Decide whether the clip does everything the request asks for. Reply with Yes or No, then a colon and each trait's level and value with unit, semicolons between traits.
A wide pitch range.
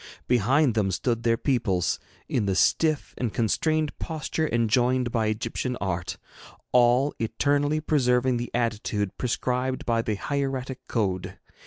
No: average, 3.3 semitones